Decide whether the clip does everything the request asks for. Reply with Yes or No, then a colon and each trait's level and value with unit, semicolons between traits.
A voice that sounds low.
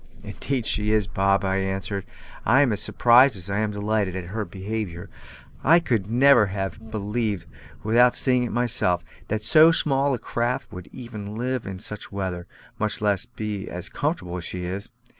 Yes: low, 105 Hz